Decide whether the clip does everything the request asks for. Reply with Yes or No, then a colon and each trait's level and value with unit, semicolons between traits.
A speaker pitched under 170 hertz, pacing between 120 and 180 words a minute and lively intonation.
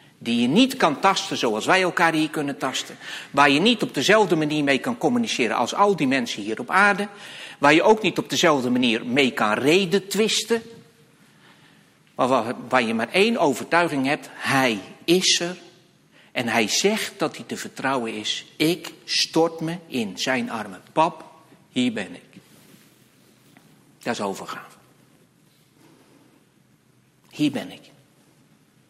No: medium, 175 Hz; average, 150 wpm; wide, 6.4 semitones